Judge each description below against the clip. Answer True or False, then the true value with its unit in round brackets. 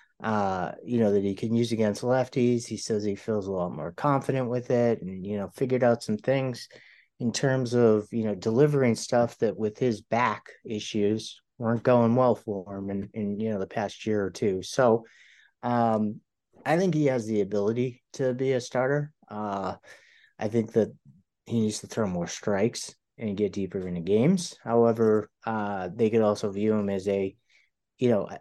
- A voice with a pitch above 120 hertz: False (110 Hz)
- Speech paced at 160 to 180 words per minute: False (190 wpm)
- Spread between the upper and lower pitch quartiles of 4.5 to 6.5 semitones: False (3.1 semitones)